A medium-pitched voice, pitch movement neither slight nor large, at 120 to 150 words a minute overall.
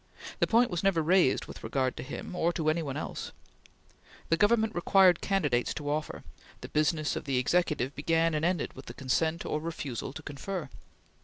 No: medium, 160 Hz; average, 3.6 semitones; average, 185 wpm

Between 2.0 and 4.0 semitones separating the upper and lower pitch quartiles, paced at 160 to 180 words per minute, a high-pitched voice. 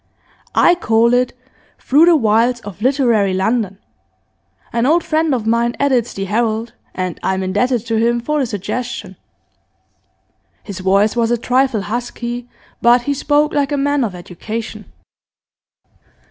No: average, 3.6 semitones; average, 145 wpm; high, 235 Hz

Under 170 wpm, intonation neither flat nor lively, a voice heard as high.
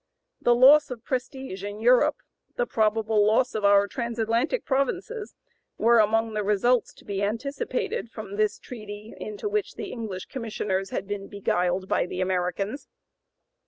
Yes: average, 155 wpm; average, 3.8 semitones; high, 220 Hz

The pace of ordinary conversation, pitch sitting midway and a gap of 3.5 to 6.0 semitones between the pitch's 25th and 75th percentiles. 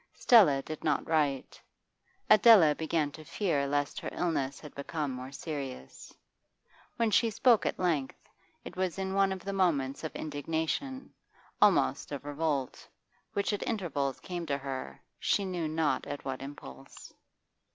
Yes: average, 150 wpm; medium, 155 Hz; average, 5.0 semitones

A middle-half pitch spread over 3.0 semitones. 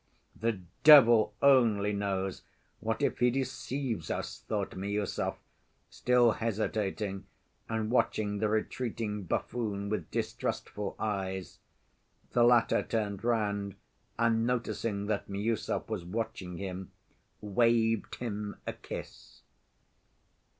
No: narrow, 2.5 semitones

